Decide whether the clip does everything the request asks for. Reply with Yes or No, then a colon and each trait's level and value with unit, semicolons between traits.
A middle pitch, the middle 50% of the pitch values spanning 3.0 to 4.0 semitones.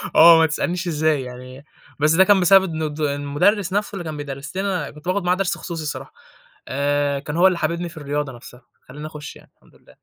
Yes: medium, 155 Hz; average, 3.6 semitones